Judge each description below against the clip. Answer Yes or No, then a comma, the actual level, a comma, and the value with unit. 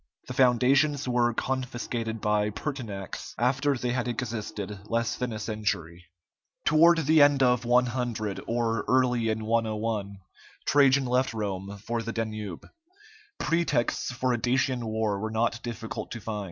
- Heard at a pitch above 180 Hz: No, low, 115 Hz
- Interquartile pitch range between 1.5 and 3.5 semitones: Yes, average, 2.8 semitones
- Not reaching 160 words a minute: Yes, average, 140 wpm